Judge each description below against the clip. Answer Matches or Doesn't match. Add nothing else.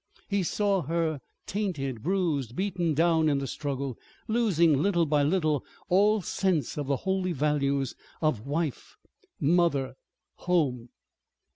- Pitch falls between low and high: Matches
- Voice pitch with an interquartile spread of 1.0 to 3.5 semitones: Doesn't match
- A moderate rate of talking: Doesn't match